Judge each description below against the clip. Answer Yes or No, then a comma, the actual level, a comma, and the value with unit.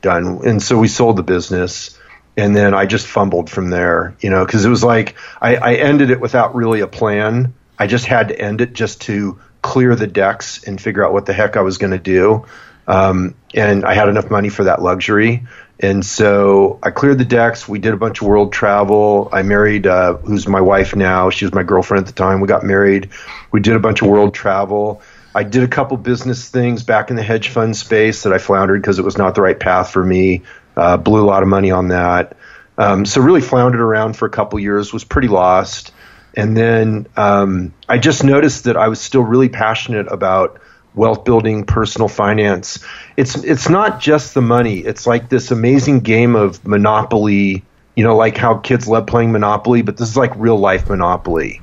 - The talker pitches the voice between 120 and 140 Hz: No, low, 105 Hz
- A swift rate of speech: Yes, fast, 215 wpm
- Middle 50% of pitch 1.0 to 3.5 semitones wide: Yes, average, 2.9 semitones